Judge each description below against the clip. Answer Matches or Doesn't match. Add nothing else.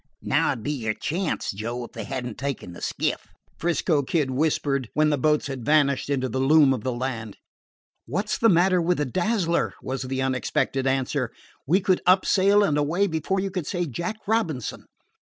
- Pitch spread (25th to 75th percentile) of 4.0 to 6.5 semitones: Matches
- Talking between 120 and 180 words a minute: Doesn't match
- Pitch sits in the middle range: Matches